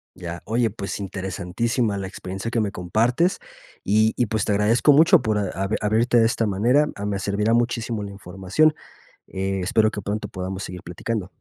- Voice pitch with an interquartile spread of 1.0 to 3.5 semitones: Yes, average, 3.1 semitones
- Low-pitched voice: Yes, low, 105 Hz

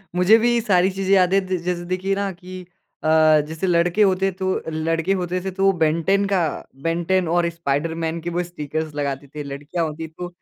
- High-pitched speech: No, medium, 175 Hz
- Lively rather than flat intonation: No, narrow, 2.6 semitones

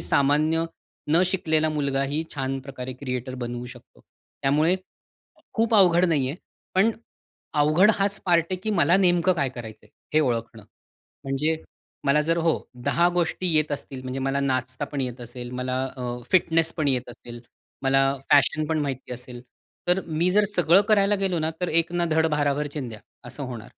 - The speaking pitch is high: No, medium, 145 Hz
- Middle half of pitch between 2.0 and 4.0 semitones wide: No, average, 4.7 semitones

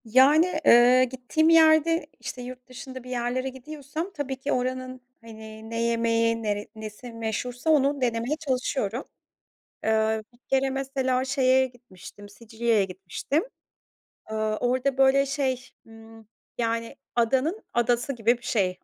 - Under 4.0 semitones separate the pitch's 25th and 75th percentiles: Yes, average, 2.9 semitones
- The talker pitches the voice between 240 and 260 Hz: Yes, very high, 250 Hz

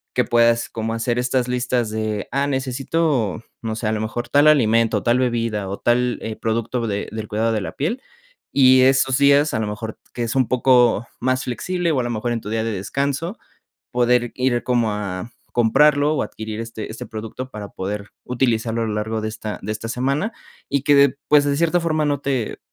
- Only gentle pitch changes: No, average, 3.4 semitones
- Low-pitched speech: Yes, low, 120 Hz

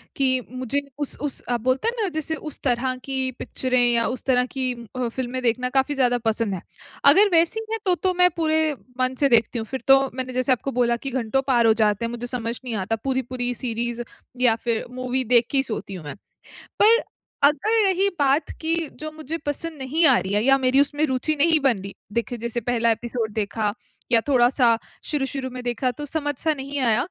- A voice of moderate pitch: No, very high, 255 Hz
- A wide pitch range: No, average, 3.3 semitones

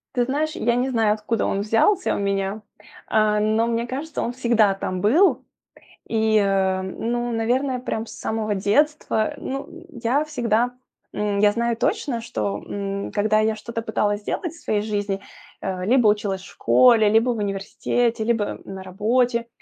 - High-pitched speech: Yes, high, 220 Hz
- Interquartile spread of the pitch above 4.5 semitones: No, average, 2.9 semitones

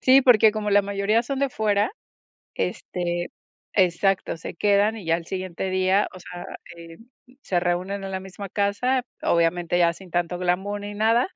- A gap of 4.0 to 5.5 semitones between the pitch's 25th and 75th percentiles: No, average, 2.9 semitones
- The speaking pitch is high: Yes, high, 195 Hz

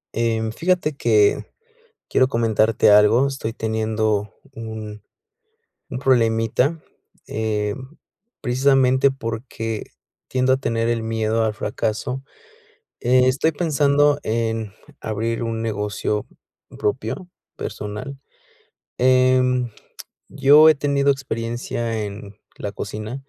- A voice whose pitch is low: Yes, low, 115 Hz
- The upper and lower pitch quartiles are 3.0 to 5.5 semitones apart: Yes, average, 3.3 semitones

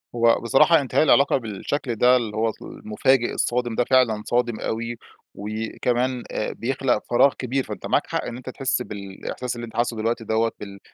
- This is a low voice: Yes, low, 120 Hz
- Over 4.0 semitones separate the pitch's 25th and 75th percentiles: No, narrow, 2.4 semitones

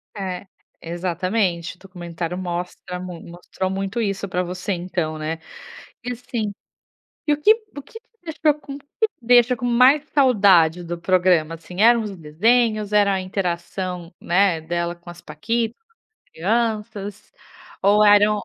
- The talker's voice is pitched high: Yes, high, 195 Hz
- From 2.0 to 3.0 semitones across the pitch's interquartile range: No, average, 4.8 semitones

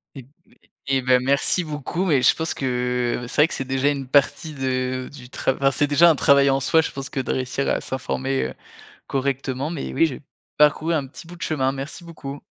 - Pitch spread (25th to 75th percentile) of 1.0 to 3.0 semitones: Yes, narrow, 2.4 semitones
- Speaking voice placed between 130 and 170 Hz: Yes, low, 135 Hz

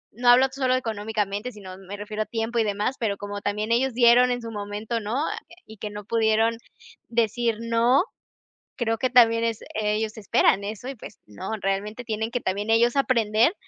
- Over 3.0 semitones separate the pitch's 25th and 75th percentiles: No, narrow, 2.4 semitones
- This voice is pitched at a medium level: No, high, 225 Hz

